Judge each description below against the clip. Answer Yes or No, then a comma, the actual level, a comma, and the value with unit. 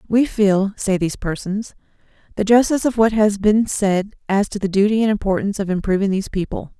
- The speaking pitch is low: No, high, 205 Hz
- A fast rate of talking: No, average, 195 wpm